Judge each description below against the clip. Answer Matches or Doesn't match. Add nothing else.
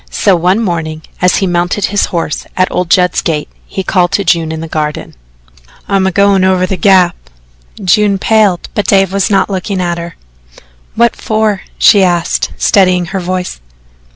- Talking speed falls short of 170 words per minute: Doesn't match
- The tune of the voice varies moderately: Doesn't match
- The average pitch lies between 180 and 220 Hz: Matches